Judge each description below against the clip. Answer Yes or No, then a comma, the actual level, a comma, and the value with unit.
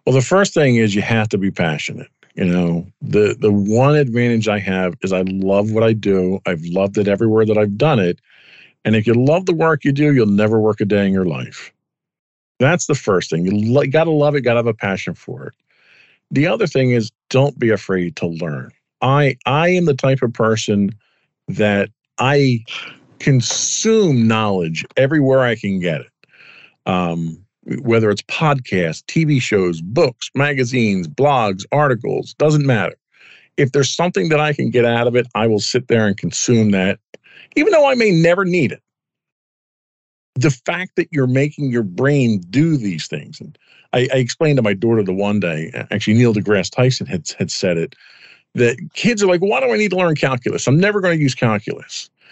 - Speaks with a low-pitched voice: Yes, low, 120 Hz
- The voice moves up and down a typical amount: No, wide, 5.8 semitones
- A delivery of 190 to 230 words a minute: Yes, average, 195 wpm